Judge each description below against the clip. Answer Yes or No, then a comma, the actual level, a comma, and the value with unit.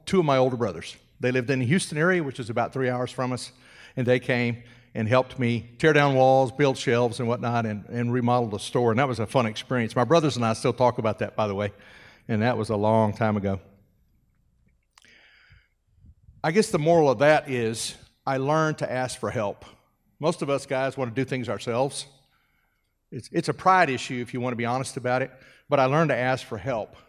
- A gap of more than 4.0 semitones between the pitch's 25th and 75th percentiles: No, average, 2.7 semitones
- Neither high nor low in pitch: No, low, 125 Hz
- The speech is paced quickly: Yes, fast, 225 wpm